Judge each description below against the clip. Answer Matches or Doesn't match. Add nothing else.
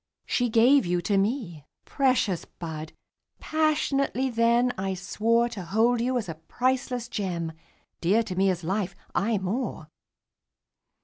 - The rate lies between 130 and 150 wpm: Matches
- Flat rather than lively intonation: Doesn't match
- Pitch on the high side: Matches